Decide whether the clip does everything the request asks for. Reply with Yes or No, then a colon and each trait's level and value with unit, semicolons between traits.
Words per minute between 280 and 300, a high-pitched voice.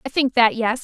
Yes: fast, 290 wpm; high, 245 Hz